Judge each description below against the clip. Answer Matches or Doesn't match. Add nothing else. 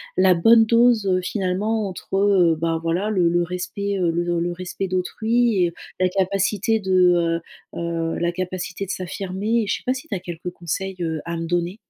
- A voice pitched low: Doesn't match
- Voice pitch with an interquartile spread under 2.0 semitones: Doesn't match